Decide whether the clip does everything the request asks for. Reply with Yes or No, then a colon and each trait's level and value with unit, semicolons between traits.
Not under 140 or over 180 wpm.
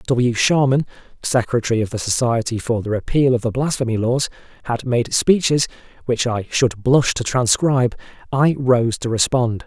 Yes: average, 160 wpm